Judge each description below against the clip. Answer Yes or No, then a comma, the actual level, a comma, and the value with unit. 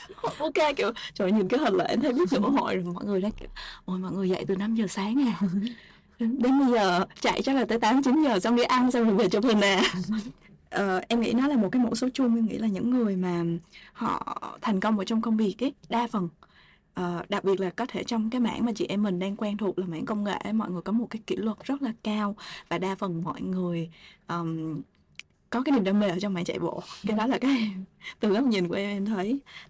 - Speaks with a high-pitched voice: Yes, high, 210 Hz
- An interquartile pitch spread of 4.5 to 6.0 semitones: No, average, 4.1 semitones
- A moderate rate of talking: No, fast, 265 wpm